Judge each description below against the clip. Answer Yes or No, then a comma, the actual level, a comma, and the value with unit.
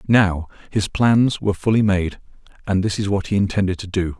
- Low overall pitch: Yes, low, 100 Hz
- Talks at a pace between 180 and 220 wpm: Yes, average, 200 wpm